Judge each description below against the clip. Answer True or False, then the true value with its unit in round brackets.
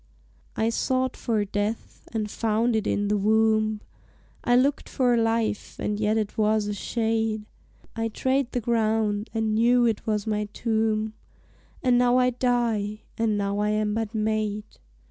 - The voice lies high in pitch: True (220 Hz)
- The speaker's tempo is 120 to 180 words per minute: True (160 wpm)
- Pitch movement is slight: True (1.7 semitones)